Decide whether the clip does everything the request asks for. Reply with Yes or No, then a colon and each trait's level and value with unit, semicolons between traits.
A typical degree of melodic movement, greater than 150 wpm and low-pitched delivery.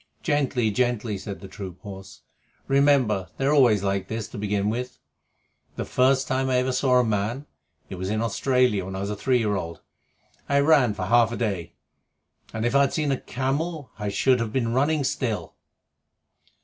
Yes: average, 4.4 semitones; average, 190 wpm; low, 120 Hz